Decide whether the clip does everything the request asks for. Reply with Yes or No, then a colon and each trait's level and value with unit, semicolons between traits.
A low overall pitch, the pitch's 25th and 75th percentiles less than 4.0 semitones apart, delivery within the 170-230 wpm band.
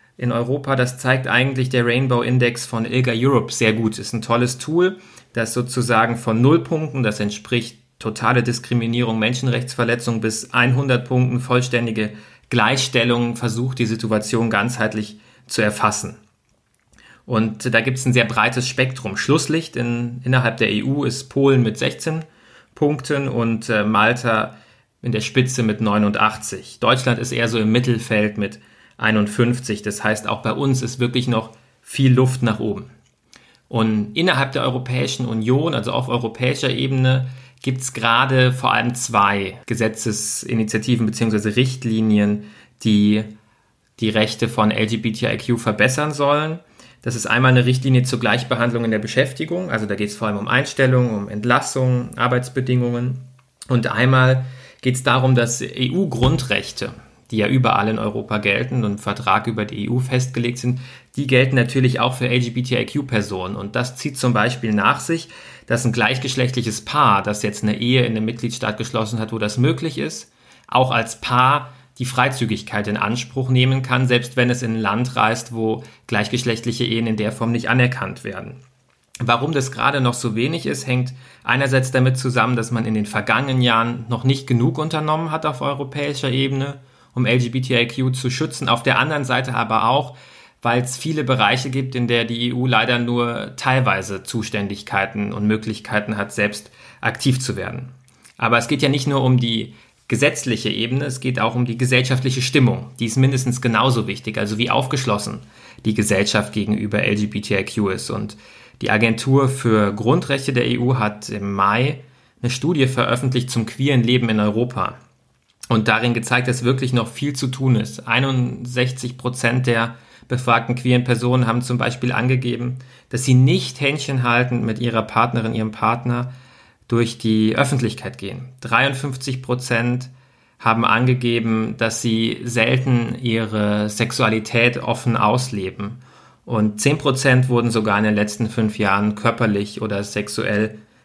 No: low, 120 Hz; narrow, 2.5 semitones; average, 155 wpm